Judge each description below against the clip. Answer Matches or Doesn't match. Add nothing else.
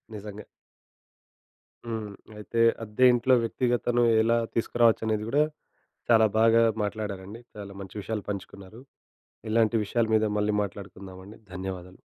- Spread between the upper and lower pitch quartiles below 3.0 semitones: Matches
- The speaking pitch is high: Doesn't match